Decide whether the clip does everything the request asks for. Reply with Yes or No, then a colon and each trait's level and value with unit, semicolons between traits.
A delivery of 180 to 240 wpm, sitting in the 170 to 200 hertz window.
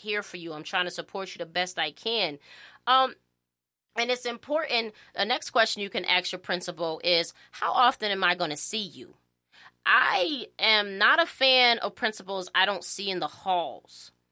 Yes: average, 190 wpm; high, 190 Hz